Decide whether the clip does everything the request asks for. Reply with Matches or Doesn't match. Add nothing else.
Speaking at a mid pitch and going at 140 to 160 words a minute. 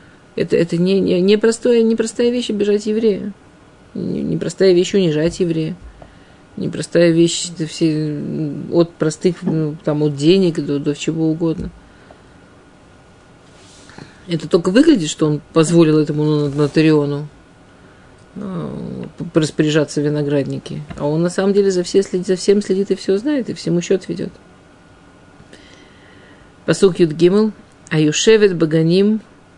Doesn't match